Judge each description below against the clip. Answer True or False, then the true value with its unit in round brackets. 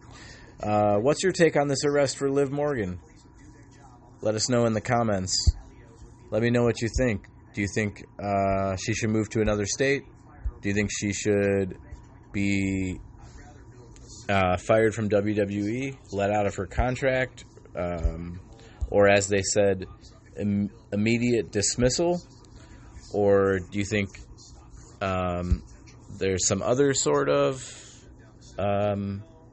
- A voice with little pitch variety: False (3.4 semitones)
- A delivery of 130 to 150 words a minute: True (135 wpm)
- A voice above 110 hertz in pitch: False (105 Hz)